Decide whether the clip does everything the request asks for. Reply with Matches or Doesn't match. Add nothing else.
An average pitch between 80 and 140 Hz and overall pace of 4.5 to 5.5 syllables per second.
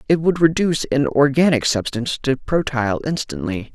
Matches